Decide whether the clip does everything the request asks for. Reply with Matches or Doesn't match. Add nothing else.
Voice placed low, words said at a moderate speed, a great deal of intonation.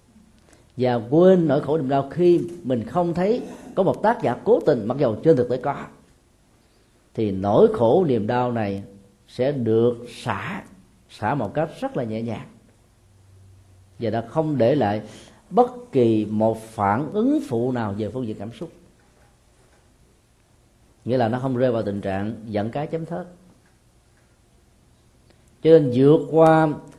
Doesn't match